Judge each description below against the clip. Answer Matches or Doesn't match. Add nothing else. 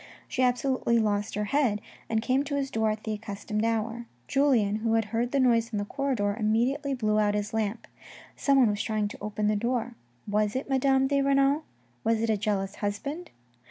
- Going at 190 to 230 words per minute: Matches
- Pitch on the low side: Doesn't match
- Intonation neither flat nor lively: Matches